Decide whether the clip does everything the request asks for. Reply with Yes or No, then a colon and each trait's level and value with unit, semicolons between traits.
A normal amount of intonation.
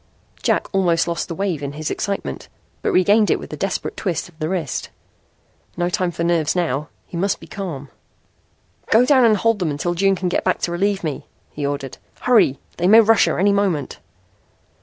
Yes: average, 4.1 semitones